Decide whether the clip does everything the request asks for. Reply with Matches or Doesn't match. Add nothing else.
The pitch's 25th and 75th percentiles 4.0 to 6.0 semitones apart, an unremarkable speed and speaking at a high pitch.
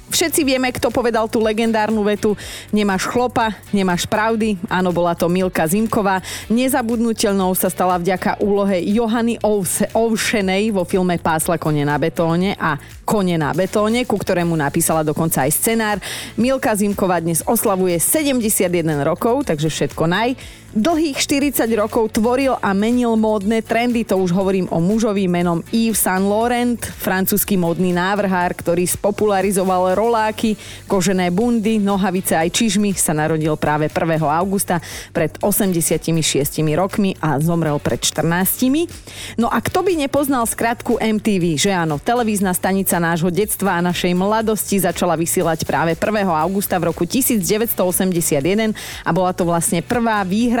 Matches